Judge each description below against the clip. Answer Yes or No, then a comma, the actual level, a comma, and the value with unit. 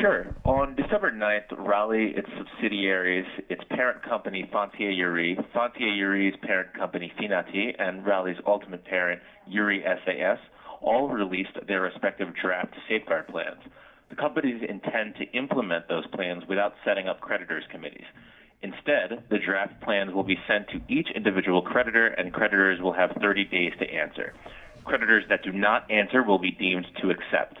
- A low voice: Yes, low, 100 Hz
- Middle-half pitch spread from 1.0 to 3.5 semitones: Yes, average, 3.0 semitones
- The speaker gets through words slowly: No, average, 155 wpm